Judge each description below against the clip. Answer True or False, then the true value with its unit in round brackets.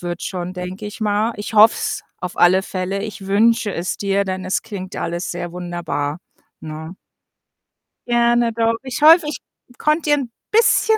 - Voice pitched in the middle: False (200 Hz)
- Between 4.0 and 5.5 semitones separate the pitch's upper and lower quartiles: True (4.5 semitones)